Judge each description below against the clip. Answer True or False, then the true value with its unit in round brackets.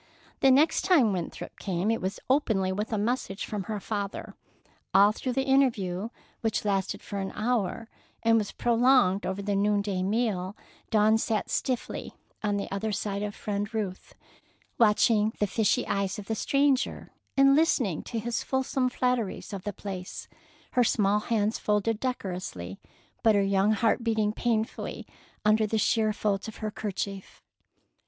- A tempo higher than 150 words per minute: True (160 wpm)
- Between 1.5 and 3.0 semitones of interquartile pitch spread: True (2.6 semitones)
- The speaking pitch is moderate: False (210 Hz)